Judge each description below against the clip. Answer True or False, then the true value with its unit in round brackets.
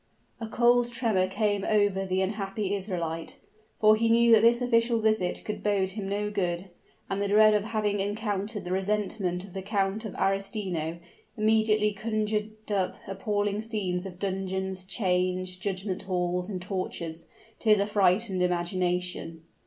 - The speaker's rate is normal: True (150 wpm)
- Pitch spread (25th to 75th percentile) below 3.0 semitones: True (2.5 semitones)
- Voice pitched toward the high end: True (200 Hz)